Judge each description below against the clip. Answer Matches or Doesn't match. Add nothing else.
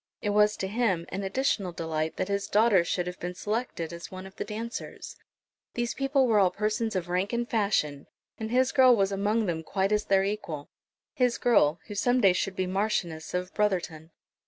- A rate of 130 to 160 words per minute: Doesn't match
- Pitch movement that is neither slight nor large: Matches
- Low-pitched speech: Doesn't match